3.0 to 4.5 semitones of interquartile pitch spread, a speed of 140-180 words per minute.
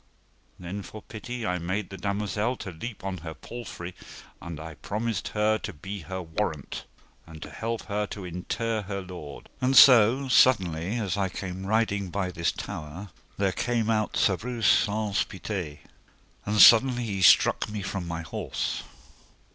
Yes: average, 3.5 semitones; average, 165 wpm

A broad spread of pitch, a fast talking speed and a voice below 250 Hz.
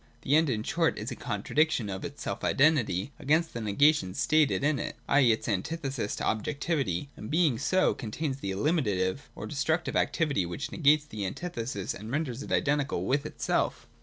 No: wide, 6.1 semitones; average, 175 wpm; medium, 140 Hz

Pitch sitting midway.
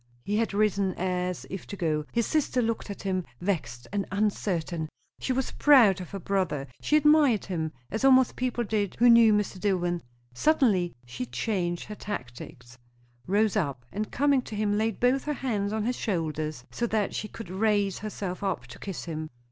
No: high, 200 Hz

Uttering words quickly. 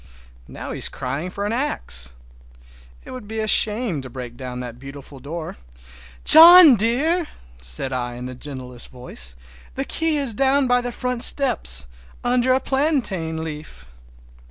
No: average, 155 wpm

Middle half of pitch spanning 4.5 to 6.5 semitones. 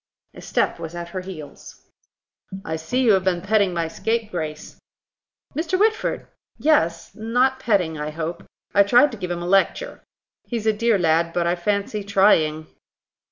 Yes: average, 5.1 semitones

